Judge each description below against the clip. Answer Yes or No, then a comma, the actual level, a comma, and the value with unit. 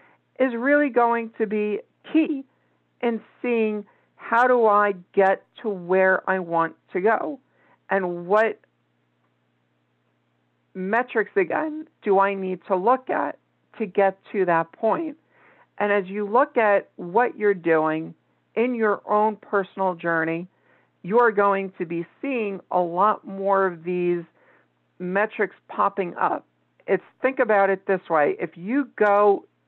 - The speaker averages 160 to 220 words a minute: No, slow, 135 wpm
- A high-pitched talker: Yes, high, 195 Hz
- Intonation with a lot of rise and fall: No, average, 4.2 semitones